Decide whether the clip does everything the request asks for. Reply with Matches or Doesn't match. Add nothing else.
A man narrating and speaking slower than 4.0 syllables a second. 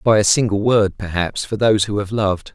Doesn't match